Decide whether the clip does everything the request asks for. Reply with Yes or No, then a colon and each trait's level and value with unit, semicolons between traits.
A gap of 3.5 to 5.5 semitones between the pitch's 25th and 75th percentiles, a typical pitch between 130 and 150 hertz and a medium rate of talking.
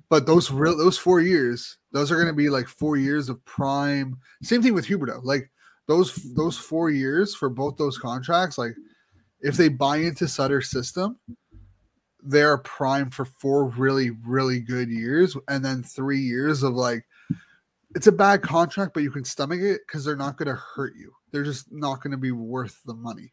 Yes: average, 3.9 semitones; medium, 140 Hz; average, 195 wpm